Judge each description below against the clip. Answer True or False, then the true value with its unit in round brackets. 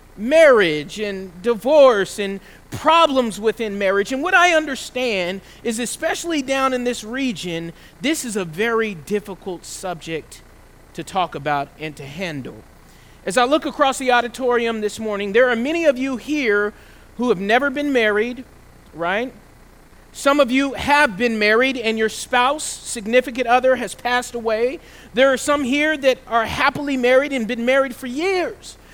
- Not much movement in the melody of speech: False (4.6 semitones)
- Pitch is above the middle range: True (245 Hz)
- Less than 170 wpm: True (160 wpm)